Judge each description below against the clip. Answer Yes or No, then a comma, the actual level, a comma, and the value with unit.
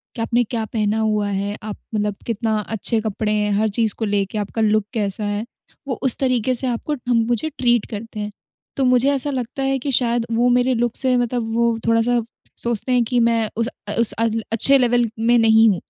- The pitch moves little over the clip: Yes, narrow, 2.3 semitones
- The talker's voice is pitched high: Yes, high, 230 Hz